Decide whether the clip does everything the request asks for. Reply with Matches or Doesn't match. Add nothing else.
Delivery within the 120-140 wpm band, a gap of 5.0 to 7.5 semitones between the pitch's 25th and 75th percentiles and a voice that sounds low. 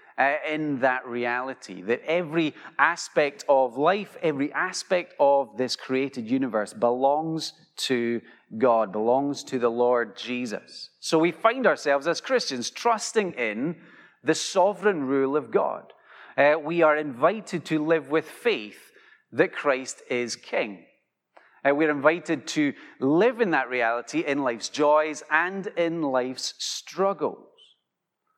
Doesn't match